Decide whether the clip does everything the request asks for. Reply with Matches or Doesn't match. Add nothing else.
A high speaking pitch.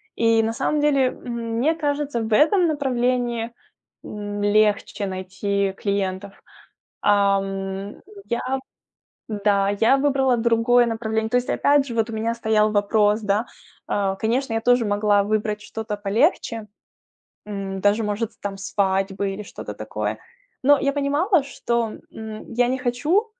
Matches